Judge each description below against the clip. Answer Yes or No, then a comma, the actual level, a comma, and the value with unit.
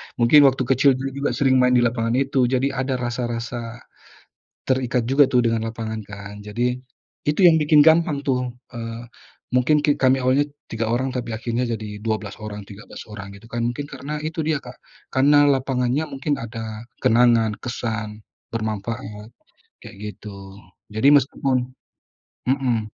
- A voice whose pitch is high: No, low, 125 Hz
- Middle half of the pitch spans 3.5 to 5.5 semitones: No, average, 3.1 semitones